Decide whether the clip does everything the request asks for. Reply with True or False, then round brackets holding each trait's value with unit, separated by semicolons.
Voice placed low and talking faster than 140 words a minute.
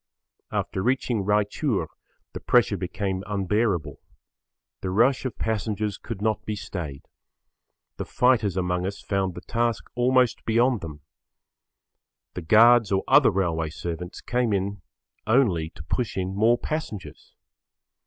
False (105 Hz; 135 wpm)